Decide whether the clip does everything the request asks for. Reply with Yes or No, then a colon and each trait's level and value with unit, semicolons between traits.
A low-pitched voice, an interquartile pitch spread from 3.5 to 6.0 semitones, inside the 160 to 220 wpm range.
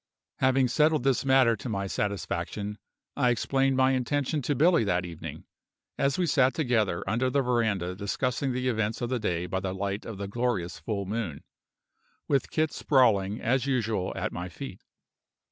Yes: low, 120 Hz; average, 5.0 semitones; average, 170 wpm